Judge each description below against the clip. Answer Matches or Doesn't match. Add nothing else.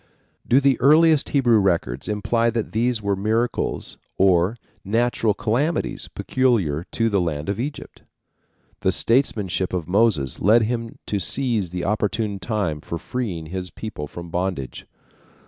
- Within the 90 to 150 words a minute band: Matches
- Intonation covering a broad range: Doesn't match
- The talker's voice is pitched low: Matches